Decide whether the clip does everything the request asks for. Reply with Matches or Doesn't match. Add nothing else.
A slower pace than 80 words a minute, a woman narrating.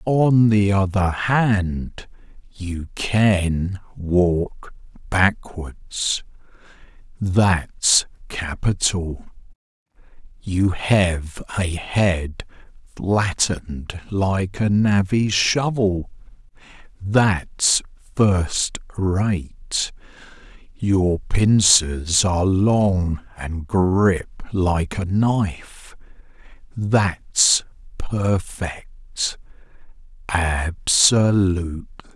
Doesn't match